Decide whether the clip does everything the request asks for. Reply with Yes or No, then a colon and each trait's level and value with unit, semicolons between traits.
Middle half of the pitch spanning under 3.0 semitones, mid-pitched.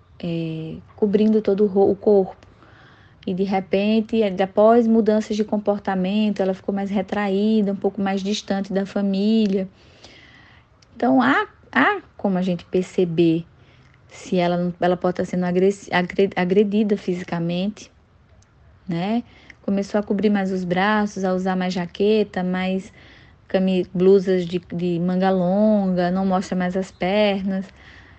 No: narrow, 2.4 semitones; high, 195 Hz